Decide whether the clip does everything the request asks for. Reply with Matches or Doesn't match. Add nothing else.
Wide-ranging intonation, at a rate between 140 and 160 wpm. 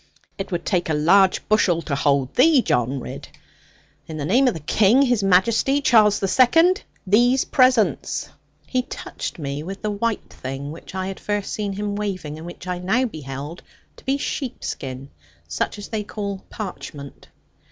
Doesn't match